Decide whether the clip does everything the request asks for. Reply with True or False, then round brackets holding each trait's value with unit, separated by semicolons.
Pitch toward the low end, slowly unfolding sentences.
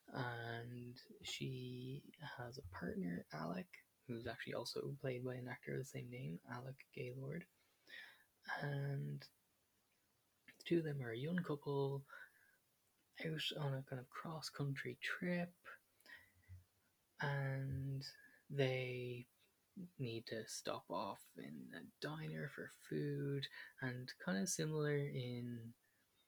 True (130 Hz; 115 wpm)